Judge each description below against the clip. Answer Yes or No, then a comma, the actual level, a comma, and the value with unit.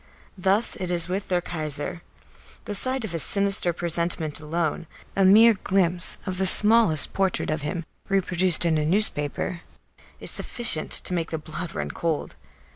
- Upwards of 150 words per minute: Yes, average, 160 wpm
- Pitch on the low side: No, medium, 175 Hz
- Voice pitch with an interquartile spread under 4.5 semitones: Yes, average, 3.3 semitones